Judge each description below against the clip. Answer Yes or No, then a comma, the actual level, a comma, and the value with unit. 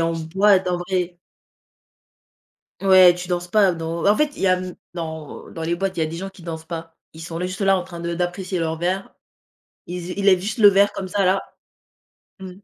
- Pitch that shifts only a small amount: Yes, narrow, 2.3 semitones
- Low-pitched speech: No, medium, 180 Hz